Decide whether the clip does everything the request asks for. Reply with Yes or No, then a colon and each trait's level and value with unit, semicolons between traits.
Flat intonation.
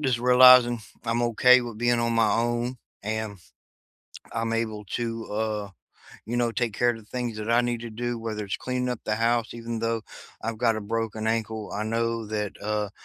Yes: narrow, 1.6 semitones